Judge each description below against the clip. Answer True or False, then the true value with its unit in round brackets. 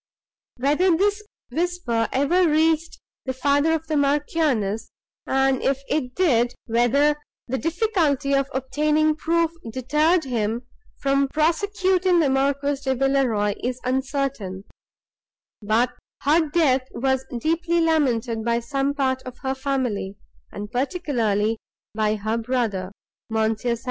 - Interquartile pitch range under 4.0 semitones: False (4.5 semitones)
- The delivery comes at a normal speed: False (125 wpm)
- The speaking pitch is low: False (270 Hz)